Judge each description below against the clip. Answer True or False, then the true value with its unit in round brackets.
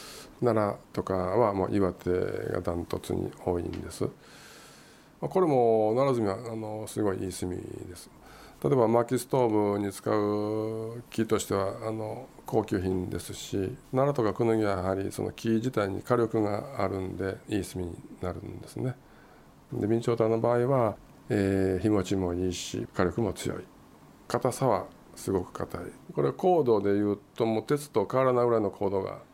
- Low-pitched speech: True (105 Hz)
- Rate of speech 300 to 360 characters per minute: True (305 characters per minute)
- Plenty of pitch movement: False (3.6 semitones)